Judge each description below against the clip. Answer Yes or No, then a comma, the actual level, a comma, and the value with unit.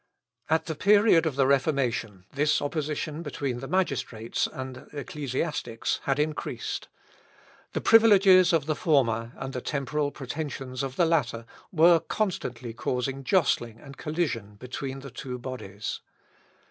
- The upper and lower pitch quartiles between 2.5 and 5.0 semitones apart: Yes, average, 4.0 semitones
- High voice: No, medium, 140 Hz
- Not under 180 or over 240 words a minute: No, slow, 135 wpm